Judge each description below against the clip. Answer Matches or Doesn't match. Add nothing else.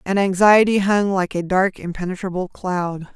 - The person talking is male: Doesn't match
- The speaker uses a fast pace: Doesn't match